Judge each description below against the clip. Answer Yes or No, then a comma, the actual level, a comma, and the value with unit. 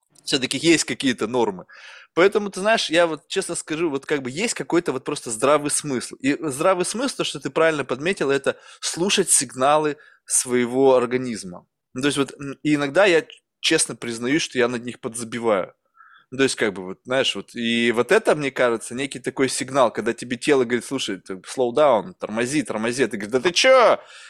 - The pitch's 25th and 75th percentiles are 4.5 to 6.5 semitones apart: Yes, average, 5.1 semitones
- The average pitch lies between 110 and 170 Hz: Yes, medium, 140 Hz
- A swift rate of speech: Yes, fast, 190 wpm